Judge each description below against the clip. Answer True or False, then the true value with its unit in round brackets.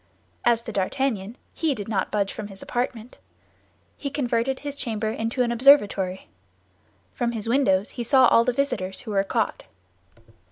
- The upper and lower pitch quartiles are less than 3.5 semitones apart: False (3.9 semitones)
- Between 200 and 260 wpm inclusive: False (160 wpm)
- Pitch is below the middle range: False (230 Hz)